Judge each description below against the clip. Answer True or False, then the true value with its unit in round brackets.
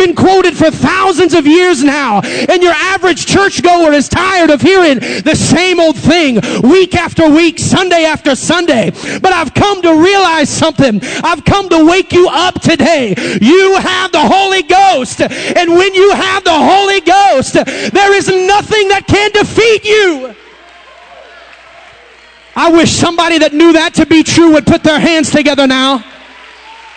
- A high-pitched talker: True (340 Hz)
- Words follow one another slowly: False (160 wpm)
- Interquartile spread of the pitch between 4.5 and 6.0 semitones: False (3.5 semitones)